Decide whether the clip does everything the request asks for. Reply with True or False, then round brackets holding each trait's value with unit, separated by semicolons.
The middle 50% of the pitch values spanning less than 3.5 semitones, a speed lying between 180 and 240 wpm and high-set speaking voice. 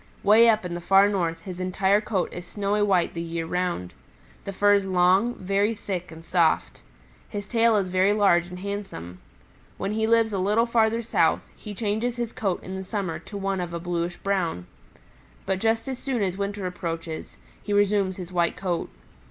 True (2.8 semitones; 195 wpm; 195 Hz)